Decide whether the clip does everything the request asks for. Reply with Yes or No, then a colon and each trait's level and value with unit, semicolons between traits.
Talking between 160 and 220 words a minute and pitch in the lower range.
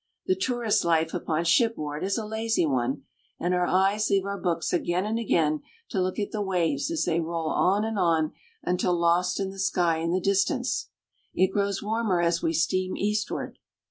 No: average, 190 wpm; medium, 185 Hz